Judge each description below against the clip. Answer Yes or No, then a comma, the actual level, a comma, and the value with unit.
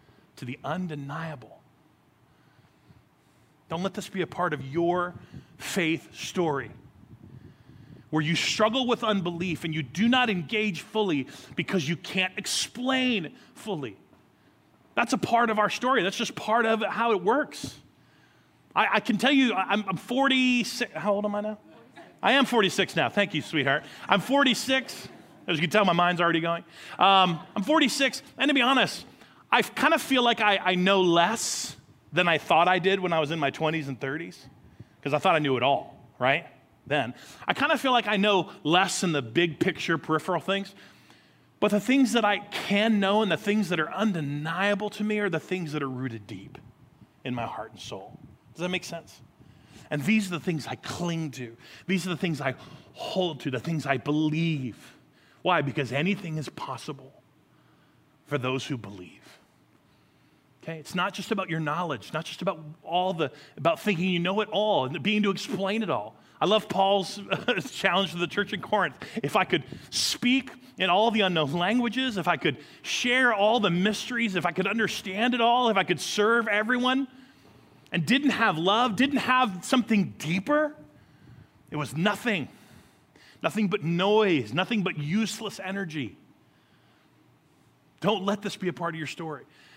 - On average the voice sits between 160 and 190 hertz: Yes, medium, 185 Hz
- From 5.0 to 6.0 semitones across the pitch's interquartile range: Yes, wide, 5.6 semitones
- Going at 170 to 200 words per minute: Yes, average, 180 wpm